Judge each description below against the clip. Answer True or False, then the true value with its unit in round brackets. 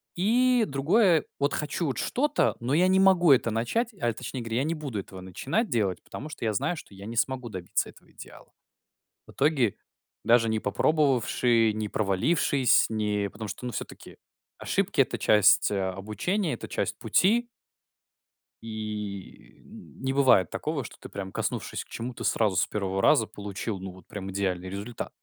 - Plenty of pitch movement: True (6.8 semitones)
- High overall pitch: False (115 Hz)